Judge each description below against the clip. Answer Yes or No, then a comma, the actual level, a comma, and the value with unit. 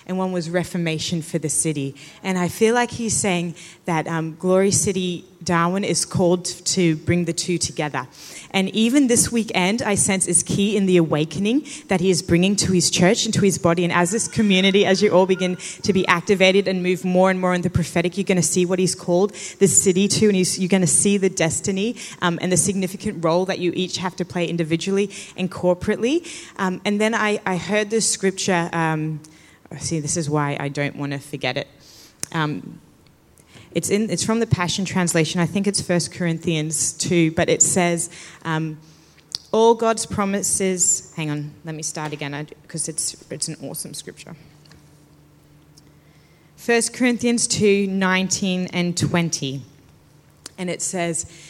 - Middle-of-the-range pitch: Yes, medium, 180 Hz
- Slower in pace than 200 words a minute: Yes, average, 185 wpm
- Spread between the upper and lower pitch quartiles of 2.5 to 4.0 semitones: Yes, average, 3.0 semitones